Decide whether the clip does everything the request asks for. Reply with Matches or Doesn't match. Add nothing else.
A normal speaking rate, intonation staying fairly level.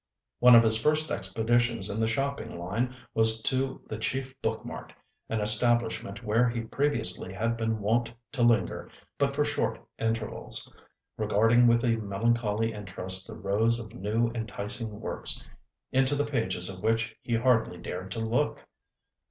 Matches